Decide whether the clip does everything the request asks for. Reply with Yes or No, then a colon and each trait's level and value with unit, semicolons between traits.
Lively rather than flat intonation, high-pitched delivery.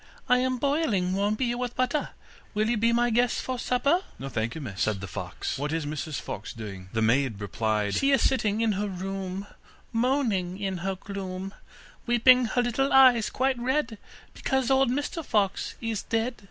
Yes: wide, 6.1 semitones; high, 215 Hz